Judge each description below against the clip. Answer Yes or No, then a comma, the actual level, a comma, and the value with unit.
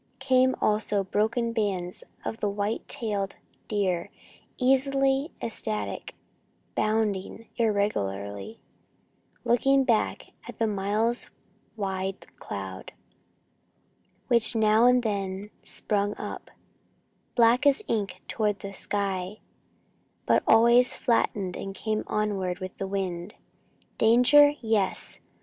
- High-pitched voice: Yes, high, 210 Hz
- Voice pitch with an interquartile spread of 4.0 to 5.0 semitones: No, average, 3.3 semitones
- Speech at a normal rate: No, slow, 100 wpm